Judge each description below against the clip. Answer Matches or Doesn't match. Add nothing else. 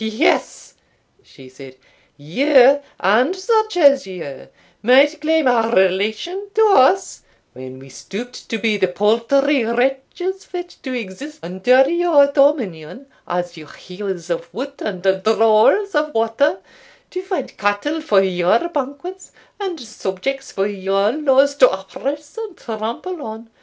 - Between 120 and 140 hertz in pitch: Doesn't match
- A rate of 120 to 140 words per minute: Matches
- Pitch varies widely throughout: Matches